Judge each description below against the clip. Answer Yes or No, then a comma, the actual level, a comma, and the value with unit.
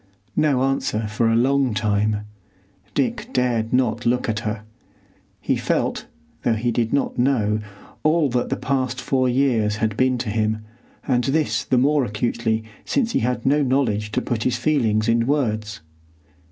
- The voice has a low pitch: Yes, low, 120 Hz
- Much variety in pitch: No, average, 3.4 semitones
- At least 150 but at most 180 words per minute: Yes, average, 165 wpm